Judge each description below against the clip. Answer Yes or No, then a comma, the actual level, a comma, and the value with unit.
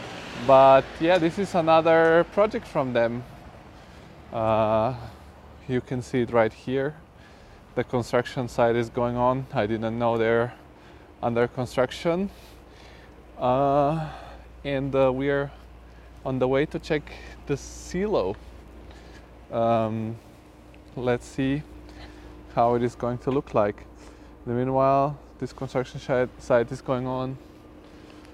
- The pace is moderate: No, slow, 120 wpm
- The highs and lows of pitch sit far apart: No, average, 3.8 semitones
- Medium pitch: No, low, 125 Hz